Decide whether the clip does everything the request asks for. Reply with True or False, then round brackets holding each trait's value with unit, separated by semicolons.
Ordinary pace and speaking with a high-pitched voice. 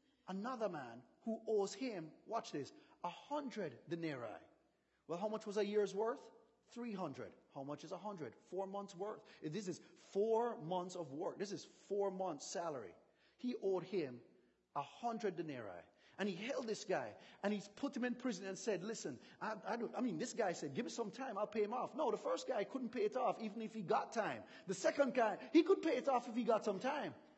False (220 wpm; 215 Hz)